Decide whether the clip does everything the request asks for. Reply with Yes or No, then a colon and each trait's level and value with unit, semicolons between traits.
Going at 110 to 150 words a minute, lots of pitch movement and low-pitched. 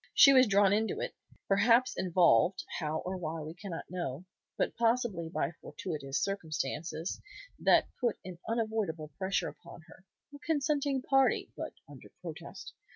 No: average, 145 wpm; wide, 6.0 semitones; high, 190 Hz